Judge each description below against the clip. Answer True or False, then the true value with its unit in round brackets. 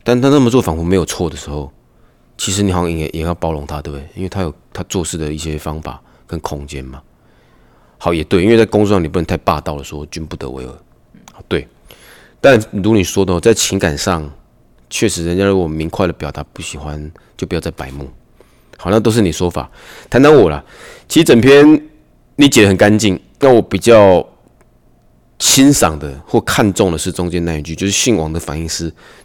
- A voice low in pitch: True (85 Hz)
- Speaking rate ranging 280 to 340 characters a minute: True (290 characters per minute)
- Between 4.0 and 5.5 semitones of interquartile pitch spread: True (4.4 semitones)